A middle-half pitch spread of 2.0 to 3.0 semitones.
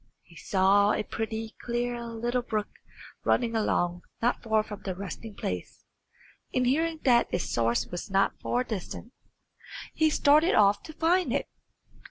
No: average, 3.7 semitones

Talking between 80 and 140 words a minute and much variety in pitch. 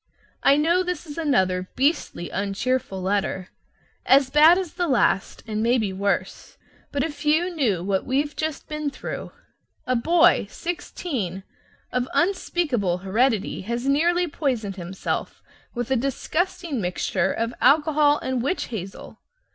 Yes: slow, 135 wpm; wide, 7.5 semitones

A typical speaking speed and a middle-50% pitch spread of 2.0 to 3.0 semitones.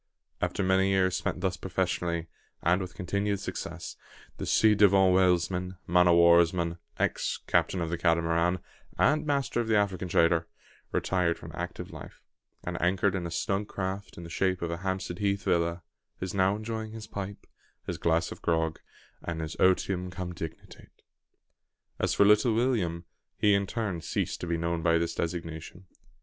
Yes: average, 170 wpm; narrow, 2.6 semitones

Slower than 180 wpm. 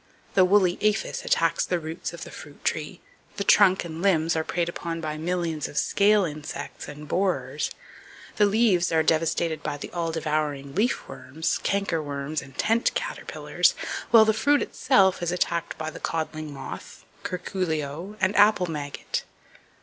Yes: average, 160 wpm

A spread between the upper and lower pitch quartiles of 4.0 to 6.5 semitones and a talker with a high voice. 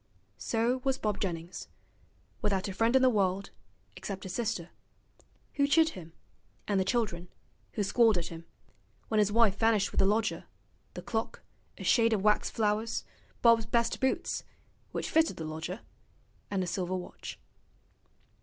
No: average, 3.6 semitones; high, 210 Hz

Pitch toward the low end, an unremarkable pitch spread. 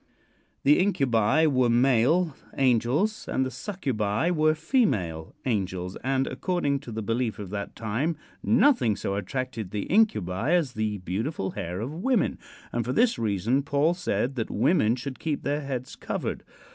No: low, 130 Hz; wide, 6.4 semitones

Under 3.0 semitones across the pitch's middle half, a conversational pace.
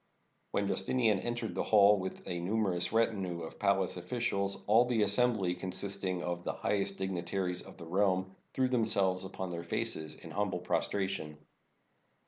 Yes: narrow, 2.6 semitones; average, 150 wpm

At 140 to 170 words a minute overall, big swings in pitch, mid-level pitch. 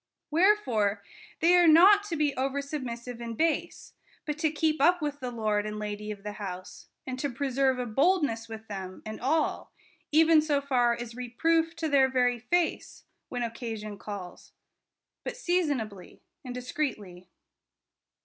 No: average, 155 wpm; wide, 5.9 semitones; very high, 255 Hz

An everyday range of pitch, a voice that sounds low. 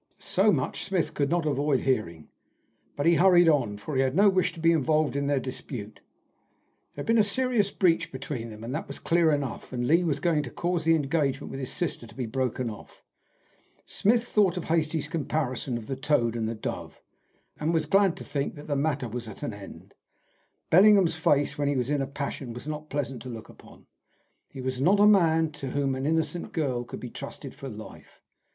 No: average, 4.2 semitones; medium, 145 Hz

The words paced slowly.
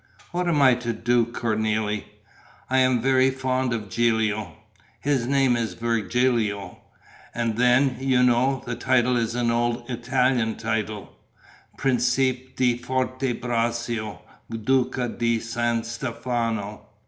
Yes: slow, 120 wpm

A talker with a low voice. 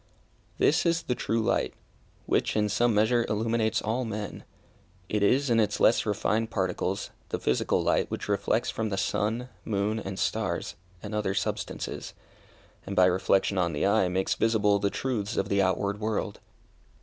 Yes: low, 105 Hz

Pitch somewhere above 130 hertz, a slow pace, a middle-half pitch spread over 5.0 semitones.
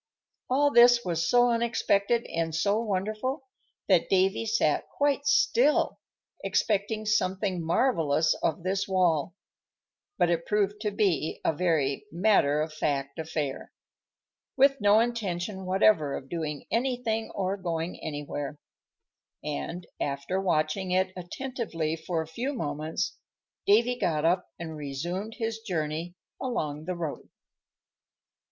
Yes: medium, 185 Hz; slow, 125 wpm; wide, 5.6 semitones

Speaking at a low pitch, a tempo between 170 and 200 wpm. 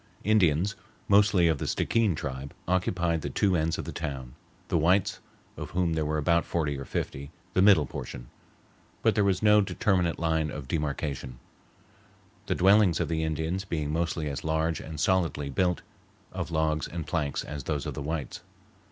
Yes: very low, 80 Hz; average, 175 wpm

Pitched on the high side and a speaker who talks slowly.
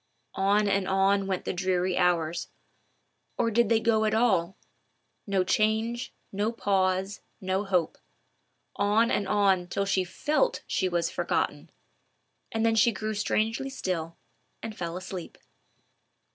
Yes: high, 195 Hz; slow, 125 wpm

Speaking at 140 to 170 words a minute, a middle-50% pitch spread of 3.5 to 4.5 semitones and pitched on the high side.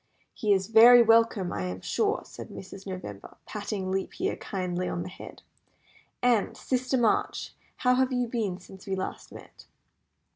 Yes: average, 160 wpm; average, 4.1 semitones; high, 200 Hz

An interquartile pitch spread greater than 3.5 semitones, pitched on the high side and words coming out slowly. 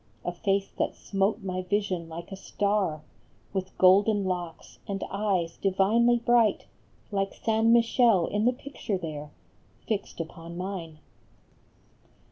No: average, 3.1 semitones; high, 195 Hz; slow, 125 wpm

